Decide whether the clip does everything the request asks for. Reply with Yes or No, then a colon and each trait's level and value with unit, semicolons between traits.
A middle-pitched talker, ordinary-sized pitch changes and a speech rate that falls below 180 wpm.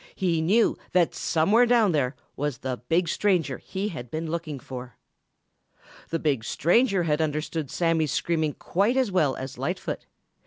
Yes: medium, 165 Hz; average, 4.3 semitones; average, 155 wpm